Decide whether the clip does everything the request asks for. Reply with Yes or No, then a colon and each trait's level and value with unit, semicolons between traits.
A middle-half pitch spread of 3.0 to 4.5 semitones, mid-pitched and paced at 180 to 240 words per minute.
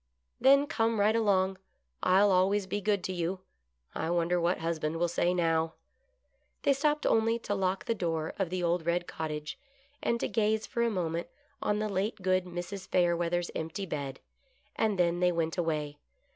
Yes: average, 3.6 semitones; medium, 180 Hz; average, 185 wpm